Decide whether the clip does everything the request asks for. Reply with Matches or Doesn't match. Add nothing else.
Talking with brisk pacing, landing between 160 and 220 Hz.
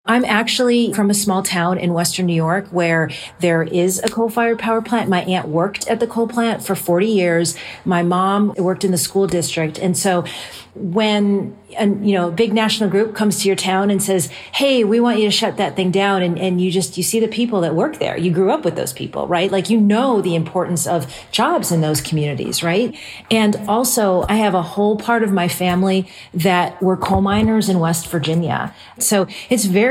Matches